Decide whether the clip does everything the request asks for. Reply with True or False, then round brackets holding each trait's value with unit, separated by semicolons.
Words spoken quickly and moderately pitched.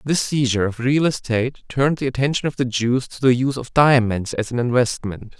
False (210 wpm; 125 Hz)